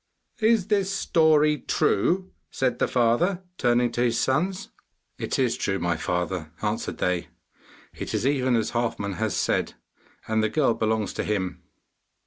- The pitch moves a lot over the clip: Yes, wide, 6.4 semitones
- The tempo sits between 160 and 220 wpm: No, average, 150 wpm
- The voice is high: No, low, 120 Hz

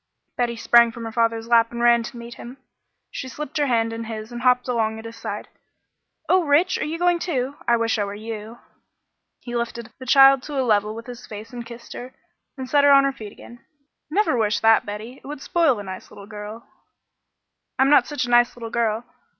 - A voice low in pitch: No, high, 235 Hz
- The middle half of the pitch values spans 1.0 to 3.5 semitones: Yes, average, 2.9 semitones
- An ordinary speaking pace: No, fast, 225 wpm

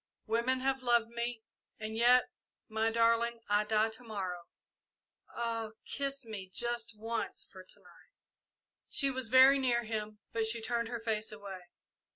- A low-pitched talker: No, high, 230 Hz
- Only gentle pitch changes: Yes, narrow, 1.8 semitones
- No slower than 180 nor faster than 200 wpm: No, average, 155 wpm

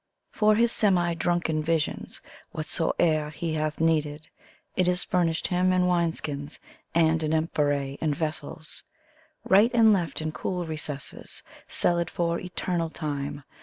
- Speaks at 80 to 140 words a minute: Yes, slow, 135 wpm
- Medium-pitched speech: Yes, medium, 165 Hz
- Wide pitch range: No, narrow, 2.5 semitones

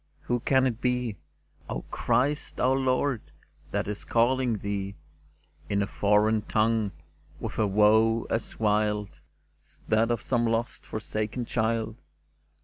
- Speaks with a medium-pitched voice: No, low, 110 Hz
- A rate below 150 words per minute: Yes, average, 140 wpm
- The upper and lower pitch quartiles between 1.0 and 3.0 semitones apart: Yes, narrow, 2.5 semitones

